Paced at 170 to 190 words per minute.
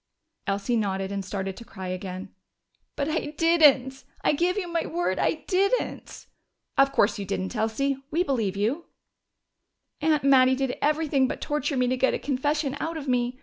Yes: average, 175 wpm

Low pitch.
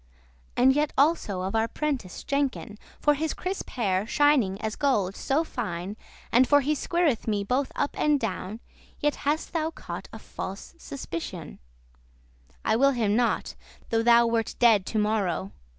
No: high, 235 Hz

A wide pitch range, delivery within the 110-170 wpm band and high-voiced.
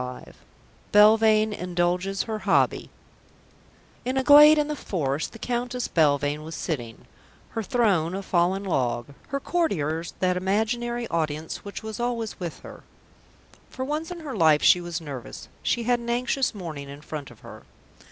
Yes: wide, 7.0 semitones; average, 160 wpm; high, 195 Hz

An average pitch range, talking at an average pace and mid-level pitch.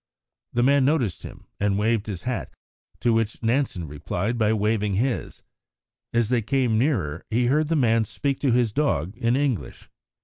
No: average, 3.8 semitones; average, 170 wpm; low, 115 Hz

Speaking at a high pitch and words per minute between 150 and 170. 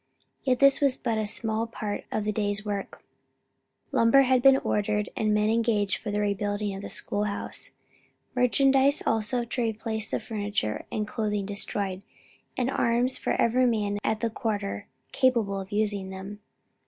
Yes: high, 215 Hz; average, 165 wpm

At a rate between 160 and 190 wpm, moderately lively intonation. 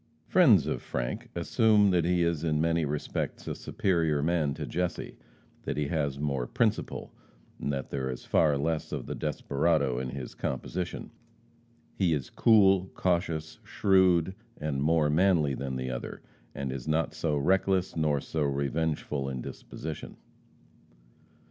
No: average, 150 wpm; average, 3.6 semitones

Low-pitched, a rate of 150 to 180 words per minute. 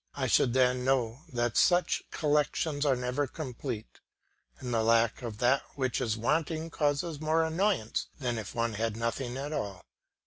Yes: low, 130 Hz; average, 170 wpm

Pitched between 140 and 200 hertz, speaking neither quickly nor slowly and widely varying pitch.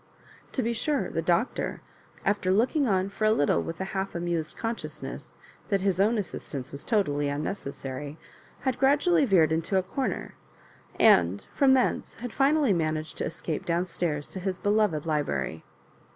Yes: high, 190 Hz; average, 170 wpm; wide, 6.4 semitones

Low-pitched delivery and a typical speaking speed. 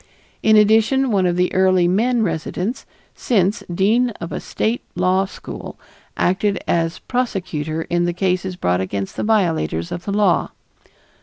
No: medium, 185 Hz; average, 150 wpm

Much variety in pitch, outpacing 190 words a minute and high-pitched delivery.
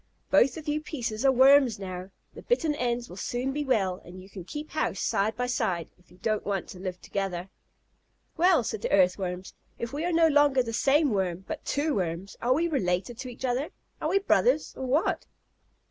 Yes: wide, 7.4 semitones; fast, 205 wpm; high, 245 Hz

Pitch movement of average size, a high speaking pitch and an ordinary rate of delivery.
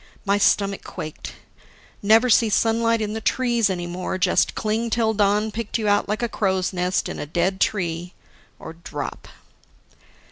Yes: average, 3.3 semitones; high, 205 Hz; average, 165 wpm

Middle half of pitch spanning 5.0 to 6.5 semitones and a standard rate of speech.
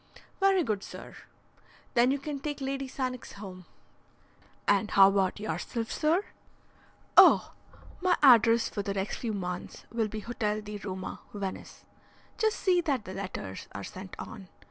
Yes: wide, 5.6 semitones; average, 150 wpm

